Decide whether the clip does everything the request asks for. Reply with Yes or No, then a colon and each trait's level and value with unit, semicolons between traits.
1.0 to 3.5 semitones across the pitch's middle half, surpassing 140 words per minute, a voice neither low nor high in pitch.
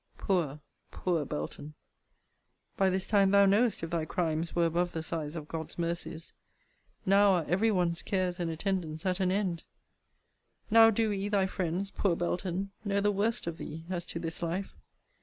Yes: average, 3.1 semitones; average, 175 wpm; medium, 180 Hz